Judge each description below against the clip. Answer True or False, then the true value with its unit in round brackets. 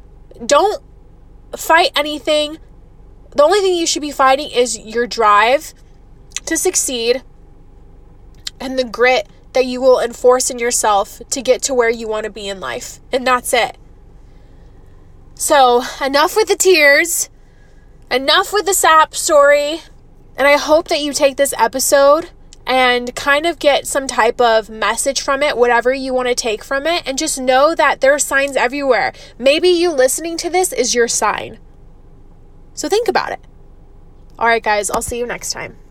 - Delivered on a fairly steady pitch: False (3.8 semitones)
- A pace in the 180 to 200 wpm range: False (165 wpm)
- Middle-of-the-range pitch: False (275 Hz)